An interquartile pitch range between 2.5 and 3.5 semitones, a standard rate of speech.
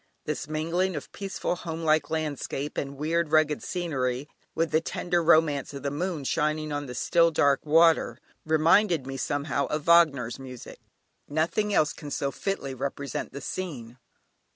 Yes: average, 3.0 semitones; average, 155 wpm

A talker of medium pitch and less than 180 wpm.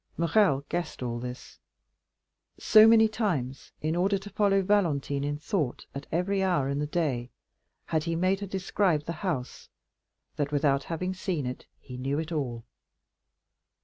Yes: medium, 160 Hz; average, 160 wpm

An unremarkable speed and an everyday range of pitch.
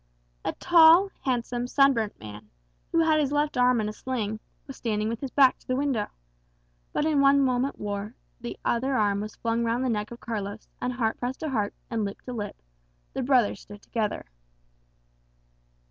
Yes: average, 185 wpm; average, 4.2 semitones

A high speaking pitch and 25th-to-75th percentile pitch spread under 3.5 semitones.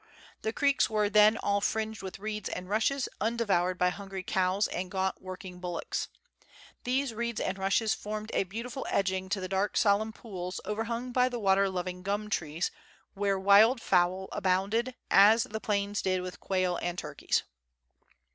Yes: high, 200 Hz; average, 2.9 semitones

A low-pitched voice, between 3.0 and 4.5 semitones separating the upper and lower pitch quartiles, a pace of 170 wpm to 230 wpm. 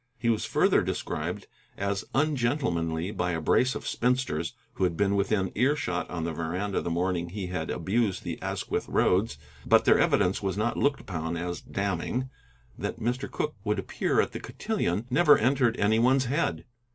No: low, 100 Hz; wide, 5.6 semitones; average, 175 wpm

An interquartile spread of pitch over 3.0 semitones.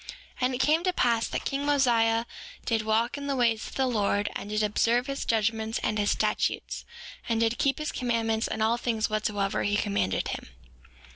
No: average, 2.7 semitones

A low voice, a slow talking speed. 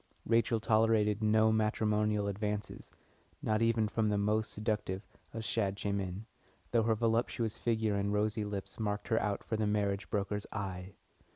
No: low, 105 Hz; average, 150 wpm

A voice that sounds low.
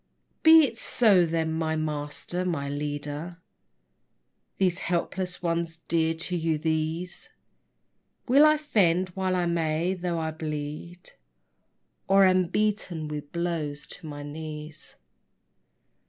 No: medium, 165 Hz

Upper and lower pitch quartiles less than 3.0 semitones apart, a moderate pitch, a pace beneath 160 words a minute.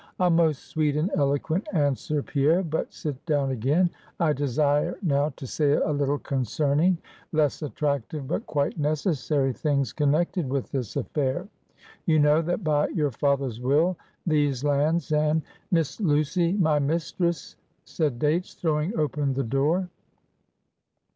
Yes: narrow, 2.5 semitones; medium, 150 Hz; average, 140 wpm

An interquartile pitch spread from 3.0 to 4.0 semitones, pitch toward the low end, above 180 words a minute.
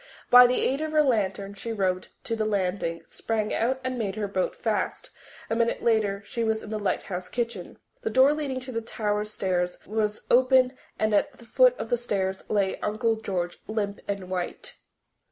No: average, 3.6 semitones; high, 215 Hz; average, 190 wpm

